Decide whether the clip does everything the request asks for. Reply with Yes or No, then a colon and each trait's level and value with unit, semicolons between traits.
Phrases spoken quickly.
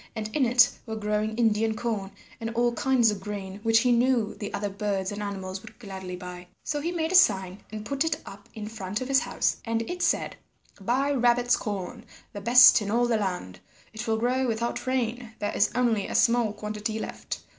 Yes: fast, 210 wpm